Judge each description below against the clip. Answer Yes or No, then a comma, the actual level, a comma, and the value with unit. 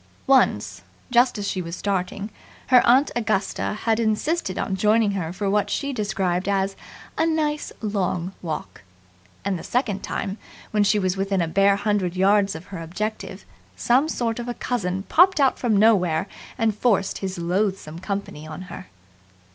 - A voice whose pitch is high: Yes, high, 200 Hz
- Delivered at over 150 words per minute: Yes, average, 165 wpm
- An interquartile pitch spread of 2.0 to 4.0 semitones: Yes, average, 3.5 semitones